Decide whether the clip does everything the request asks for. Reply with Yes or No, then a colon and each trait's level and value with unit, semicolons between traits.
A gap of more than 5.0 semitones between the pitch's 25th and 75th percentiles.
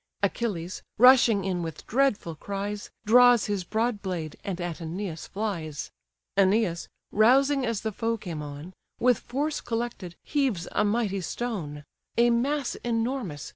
Yes: wide, 5.4 semitones